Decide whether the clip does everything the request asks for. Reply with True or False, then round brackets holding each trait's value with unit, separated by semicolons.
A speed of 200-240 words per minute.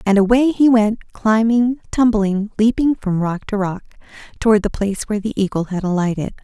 False (175 wpm)